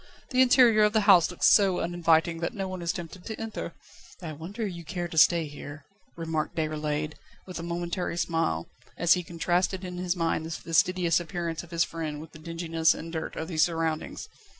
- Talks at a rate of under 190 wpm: No, average, 195 wpm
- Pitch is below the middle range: No, medium, 170 Hz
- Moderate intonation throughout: No, narrow, 2.0 semitones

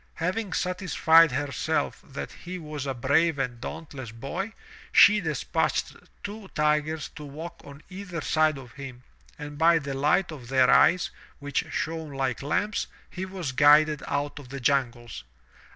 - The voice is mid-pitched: Yes, medium, 150 Hz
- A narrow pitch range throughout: No, average, 3.5 semitones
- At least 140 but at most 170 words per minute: Yes, average, 150 wpm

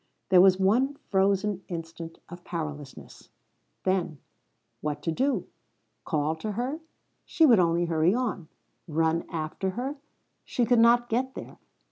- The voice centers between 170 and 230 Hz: Yes, medium, 185 Hz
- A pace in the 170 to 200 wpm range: No, slow, 135 wpm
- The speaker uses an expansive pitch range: Yes, wide, 6.4 semitones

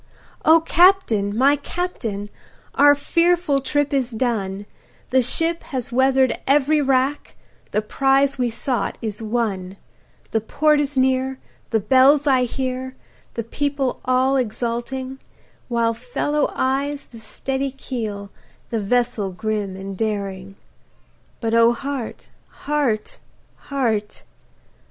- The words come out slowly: Yes, slow, 120 wpm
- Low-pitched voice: No, very high, 255 Hz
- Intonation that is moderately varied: Yes, average, 4.0 semitones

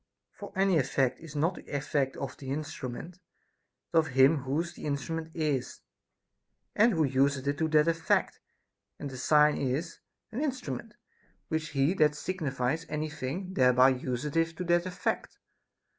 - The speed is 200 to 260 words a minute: No, average, 155 wpm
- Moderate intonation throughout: Yes, average, 3.5 semitones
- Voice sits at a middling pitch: Yes, medium, 150 Hz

